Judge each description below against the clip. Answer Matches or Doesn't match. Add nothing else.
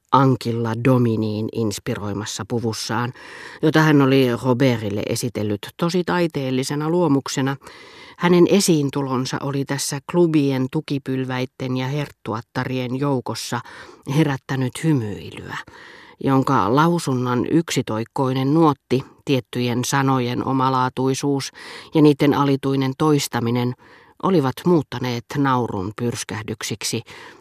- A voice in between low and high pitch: Doesn't match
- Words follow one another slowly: Matches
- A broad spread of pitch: Doesn't match